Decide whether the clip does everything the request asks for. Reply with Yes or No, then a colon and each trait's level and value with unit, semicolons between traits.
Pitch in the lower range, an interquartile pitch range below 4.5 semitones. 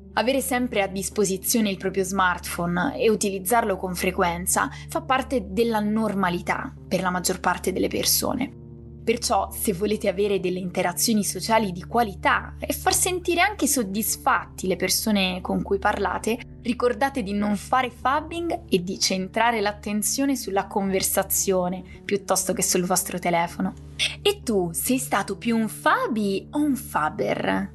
No: high, 200 Hz; average, 3.9 semitones